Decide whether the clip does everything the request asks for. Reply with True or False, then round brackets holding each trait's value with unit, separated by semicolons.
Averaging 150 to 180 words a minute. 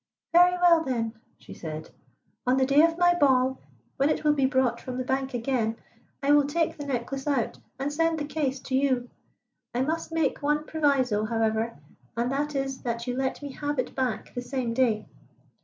False (195 wpm)